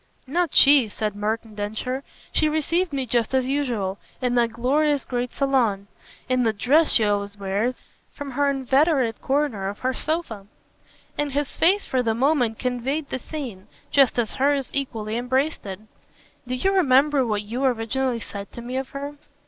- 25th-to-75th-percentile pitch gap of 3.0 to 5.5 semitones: Yes, average, 4.1 semitones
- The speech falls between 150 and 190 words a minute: Yes, average, 170 wpm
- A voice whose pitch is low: No, very high, 255 Hz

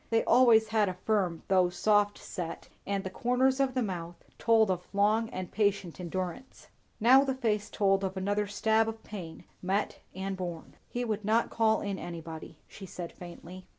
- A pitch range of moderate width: Yes, average, 3.4 semitones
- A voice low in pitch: No, high, 200 Hz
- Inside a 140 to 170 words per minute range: No, average, 180 wpm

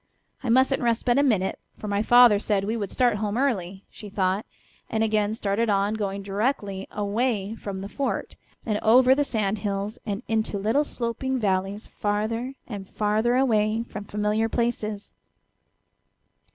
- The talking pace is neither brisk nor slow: Yes, average, 155 wpm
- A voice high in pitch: Yes, high, 215 Hz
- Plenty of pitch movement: No, average, 2.7 semitones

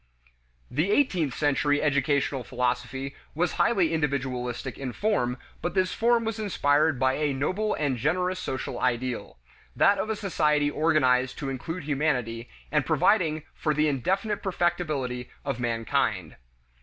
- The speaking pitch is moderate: Yes, medium, 145 Hz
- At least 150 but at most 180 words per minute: No, slow, 135 wpm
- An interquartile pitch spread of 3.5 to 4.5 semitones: No, wide, 5.5 semitones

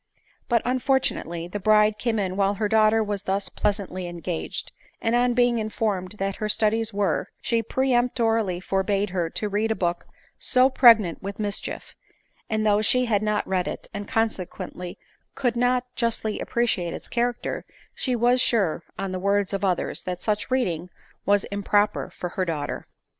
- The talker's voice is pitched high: Yes, high, 210 Hz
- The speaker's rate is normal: Yes, average, 165 wpm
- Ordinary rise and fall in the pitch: Yes, average, 3.4 semitones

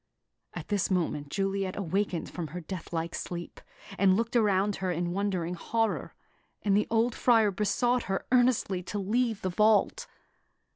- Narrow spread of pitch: No, average, 3.6 semitones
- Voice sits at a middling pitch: No, high, 195 Hz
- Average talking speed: Yes, average, 155 wpm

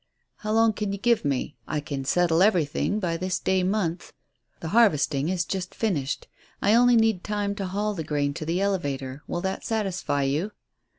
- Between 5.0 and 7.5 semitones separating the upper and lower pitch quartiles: Yes, wide, 5.4 semitones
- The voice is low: No, medium, 185 Hz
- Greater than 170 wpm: Yes, average, 185 wpm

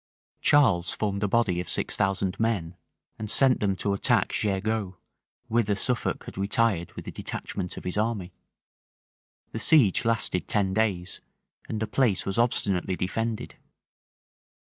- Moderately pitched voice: No, low, 100 Hz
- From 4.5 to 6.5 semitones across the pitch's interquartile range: No, average, 3.1 semitones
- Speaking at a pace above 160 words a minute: No, average, 140 wpm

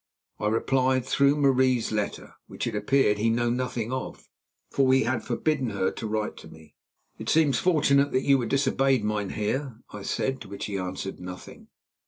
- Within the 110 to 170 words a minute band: No, average, 180 wpm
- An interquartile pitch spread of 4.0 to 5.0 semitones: Yes, average, 4.3 semitones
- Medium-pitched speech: No, low, 125 Hz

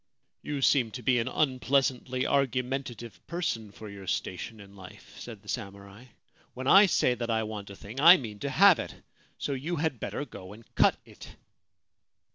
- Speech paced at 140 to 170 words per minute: No, average, 190 wpm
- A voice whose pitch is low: Yes, low, 125 Hz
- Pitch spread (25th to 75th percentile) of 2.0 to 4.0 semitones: No, average, 4.7 semitones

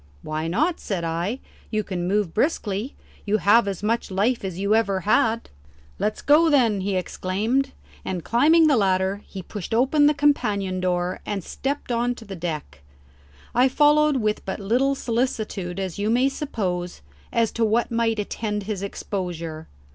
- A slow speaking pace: No, average, 165 wpm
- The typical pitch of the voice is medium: No, high, 210 Hz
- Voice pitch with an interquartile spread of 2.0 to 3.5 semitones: No, average, 4.6 semitones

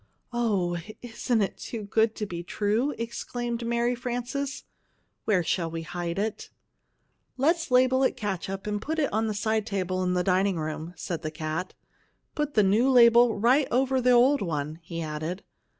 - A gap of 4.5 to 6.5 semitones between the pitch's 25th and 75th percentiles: Yes, average, 5.3 semitones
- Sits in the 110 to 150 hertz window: No, high, 215 Hz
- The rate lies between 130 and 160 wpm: No, average, 170 wpm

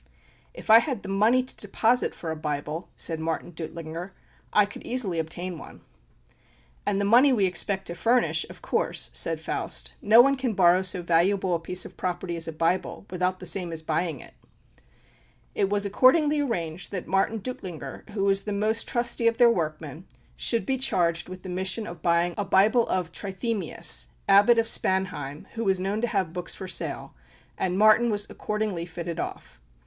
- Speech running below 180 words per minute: No, average, 185 wpm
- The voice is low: No, high, 190 Hz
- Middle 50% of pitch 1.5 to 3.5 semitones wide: No, average, 4.2 semitones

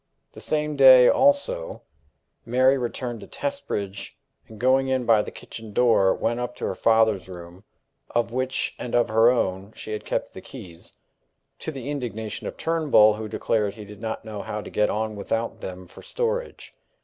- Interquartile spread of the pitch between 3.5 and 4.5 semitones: Yes, average, 3.8 semitones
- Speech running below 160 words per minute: No, average, 180 wpm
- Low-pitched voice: Yes, low, 115 Hz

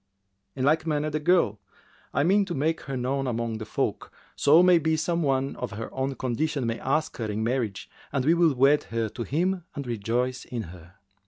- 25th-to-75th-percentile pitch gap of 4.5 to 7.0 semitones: Yes, average, 5.1 semitones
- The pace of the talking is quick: Yes, fast, 210 wpm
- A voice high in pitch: No, low, 135 Hz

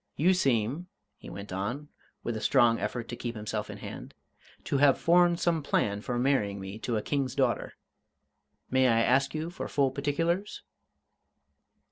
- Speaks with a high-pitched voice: No, low, 130 Hz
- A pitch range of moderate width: Yes, average, 4.6 semitones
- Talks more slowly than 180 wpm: Yes, average, 165 wpm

